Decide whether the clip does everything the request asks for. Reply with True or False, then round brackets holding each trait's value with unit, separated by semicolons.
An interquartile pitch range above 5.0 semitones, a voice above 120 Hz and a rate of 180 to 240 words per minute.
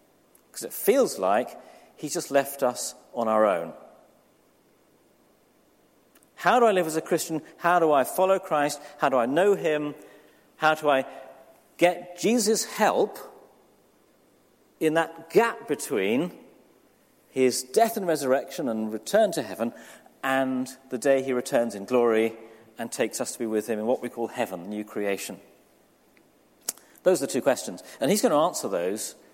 False (5.6 semitones; 135 Hz; 160 wpm)